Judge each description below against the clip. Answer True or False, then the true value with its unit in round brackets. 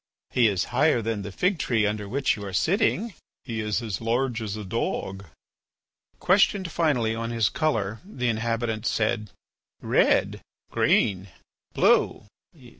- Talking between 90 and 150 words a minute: True (140 wpm)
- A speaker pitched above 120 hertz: False (115 Hz)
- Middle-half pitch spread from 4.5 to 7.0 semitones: False (4.1 semitones)